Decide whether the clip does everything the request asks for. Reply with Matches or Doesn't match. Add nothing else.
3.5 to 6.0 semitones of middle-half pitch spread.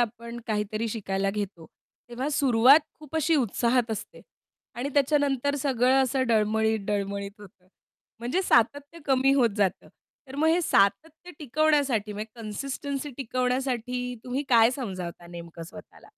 Matches